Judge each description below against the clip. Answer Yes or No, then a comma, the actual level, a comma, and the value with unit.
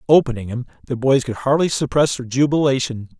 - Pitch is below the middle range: Yes, low, 130 Hz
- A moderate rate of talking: Yes, average, 170 wpm